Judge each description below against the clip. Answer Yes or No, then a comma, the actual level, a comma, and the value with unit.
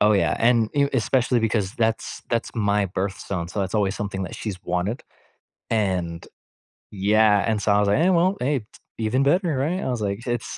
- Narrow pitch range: No, average, 3.9 semitones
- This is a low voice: Yes, low, 110 Hz